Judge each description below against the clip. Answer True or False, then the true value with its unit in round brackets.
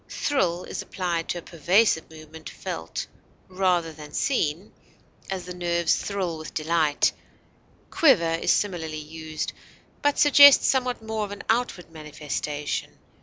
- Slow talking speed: True (125 wpm)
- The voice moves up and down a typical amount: True (4.4 semitones)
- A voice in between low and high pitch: True (170 Hz)